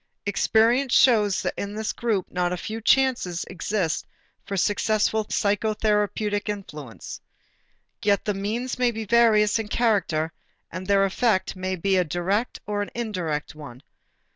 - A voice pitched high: Yes, high, 205 Hz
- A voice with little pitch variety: No, average, 3.0 semitones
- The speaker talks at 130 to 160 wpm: Yes, average, 140 wpm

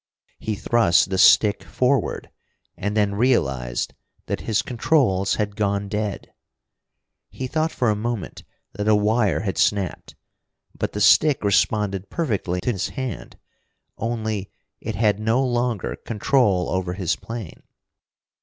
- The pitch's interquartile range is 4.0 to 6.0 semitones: No, average, 3.5 semitones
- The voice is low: Yes, low, 105 Hz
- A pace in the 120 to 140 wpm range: Yes, slow, 135 wpm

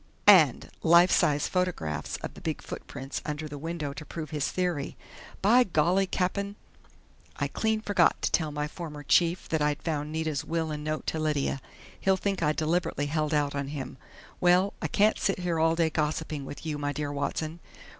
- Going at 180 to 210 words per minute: Yes, average, 185 wpm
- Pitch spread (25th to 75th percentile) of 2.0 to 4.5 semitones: Yes, average, 3.1 semitones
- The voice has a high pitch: No, medium, 155 Hz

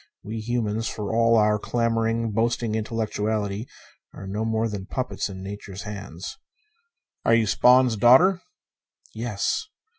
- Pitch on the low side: Yes, low, 110 Hz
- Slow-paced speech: Yes, slow, 125 wpm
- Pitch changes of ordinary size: No, narrow, 2.0 semitones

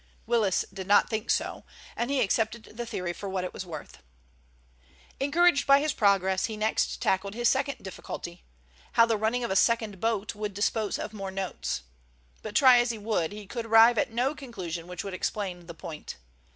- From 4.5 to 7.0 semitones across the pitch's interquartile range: No, average, 3.7 semitones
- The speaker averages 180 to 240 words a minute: Yes, average, 190 wpm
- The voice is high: Yes, high, 210 Hz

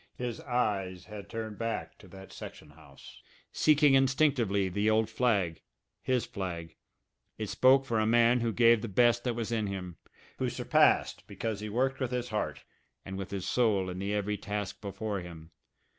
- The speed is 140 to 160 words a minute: No, average, 175 wpm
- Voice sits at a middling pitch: No, low, 110 Hz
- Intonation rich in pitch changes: No, average, 3.7 semitones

